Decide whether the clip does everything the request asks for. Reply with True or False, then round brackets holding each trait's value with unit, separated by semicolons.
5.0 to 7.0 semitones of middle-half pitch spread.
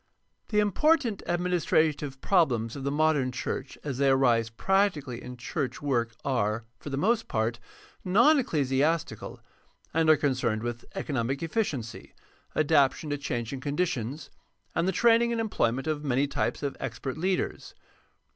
True (5.6 semitones)